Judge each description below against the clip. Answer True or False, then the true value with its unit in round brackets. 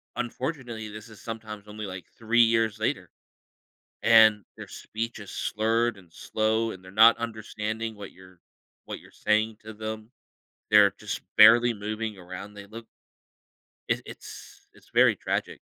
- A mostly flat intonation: True (1.5 semitones)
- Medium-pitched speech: False (110 Hz)